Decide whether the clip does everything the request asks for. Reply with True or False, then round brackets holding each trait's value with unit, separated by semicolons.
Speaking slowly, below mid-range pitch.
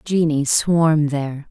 False (120 wpm; 155 Hz)